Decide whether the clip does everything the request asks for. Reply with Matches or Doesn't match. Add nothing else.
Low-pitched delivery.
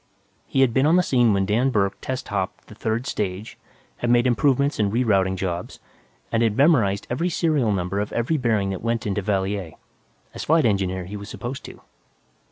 Matches